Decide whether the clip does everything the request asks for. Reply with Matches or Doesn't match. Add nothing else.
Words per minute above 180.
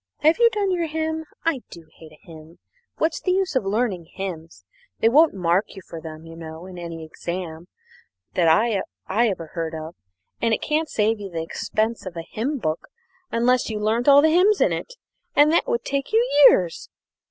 Matches